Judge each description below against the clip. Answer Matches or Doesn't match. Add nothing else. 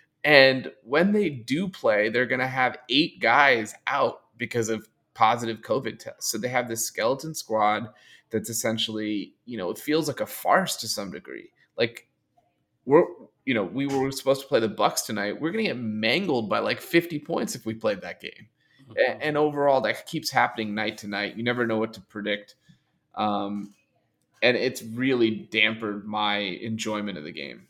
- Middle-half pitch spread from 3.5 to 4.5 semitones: Matches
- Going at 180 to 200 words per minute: Matches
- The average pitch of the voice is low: Matches